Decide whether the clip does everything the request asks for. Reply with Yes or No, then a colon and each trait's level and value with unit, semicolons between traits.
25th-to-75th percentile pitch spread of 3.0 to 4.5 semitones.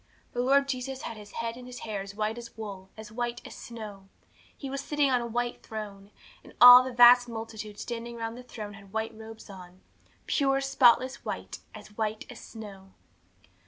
No: narrow, 2.6 semitones